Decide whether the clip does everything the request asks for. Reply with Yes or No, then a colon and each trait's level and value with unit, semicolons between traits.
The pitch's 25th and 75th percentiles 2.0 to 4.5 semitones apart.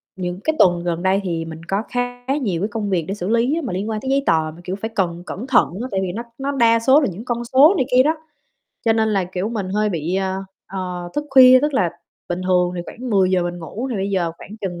No: wide, 5.4 semitones